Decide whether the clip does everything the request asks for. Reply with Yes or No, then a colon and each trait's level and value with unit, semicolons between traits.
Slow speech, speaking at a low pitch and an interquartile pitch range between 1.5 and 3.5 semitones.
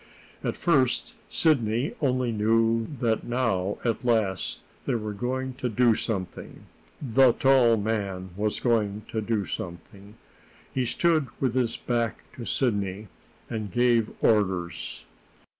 Yes: slow, 125 wpm; low, 115 Hz; average, 3.1 semitones